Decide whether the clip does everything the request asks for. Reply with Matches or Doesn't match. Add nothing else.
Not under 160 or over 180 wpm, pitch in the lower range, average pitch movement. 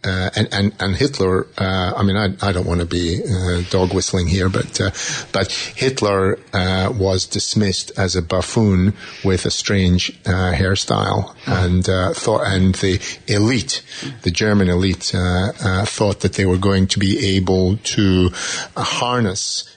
Doesn't match